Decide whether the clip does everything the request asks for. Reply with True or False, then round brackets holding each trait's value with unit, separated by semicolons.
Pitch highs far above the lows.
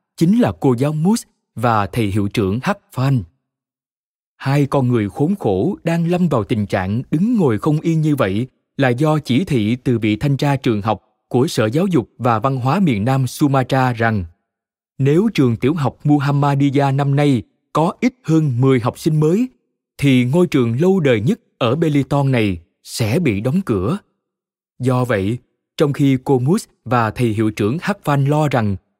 False (4.8 semitones)